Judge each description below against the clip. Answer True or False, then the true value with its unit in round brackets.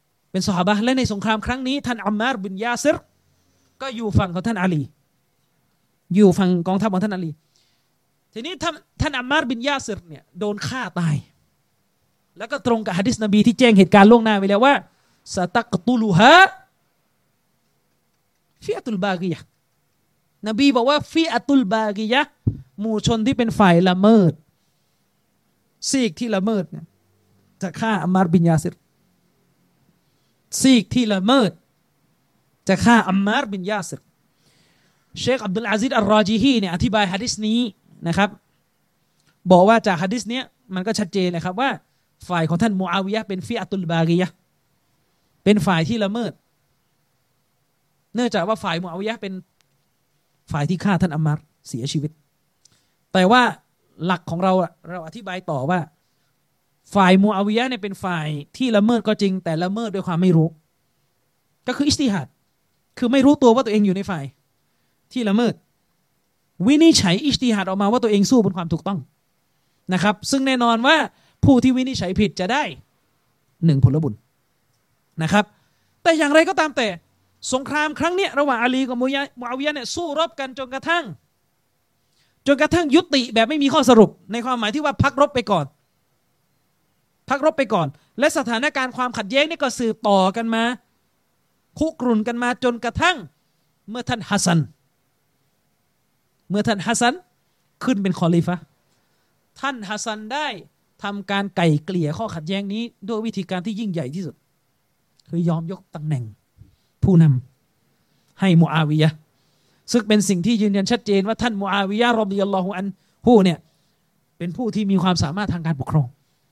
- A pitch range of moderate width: False (5.9 semitones)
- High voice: True (205 Hz)